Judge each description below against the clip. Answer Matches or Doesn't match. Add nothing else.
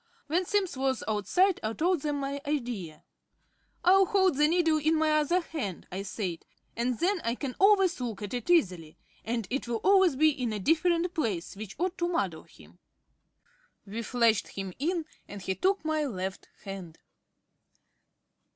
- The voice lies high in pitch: Matches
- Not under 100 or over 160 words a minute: Doesn't match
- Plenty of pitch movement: Matches